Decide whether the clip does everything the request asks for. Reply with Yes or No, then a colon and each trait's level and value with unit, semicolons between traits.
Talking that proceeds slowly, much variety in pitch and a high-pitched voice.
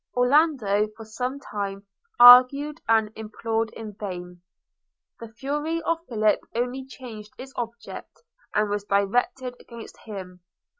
No: slow, 120 wpm; average, 3.7 semitones; high, 230 Hz